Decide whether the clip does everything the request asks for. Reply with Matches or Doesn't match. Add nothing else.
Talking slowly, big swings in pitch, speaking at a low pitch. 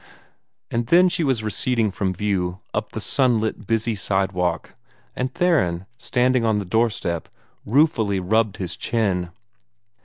Doesn't match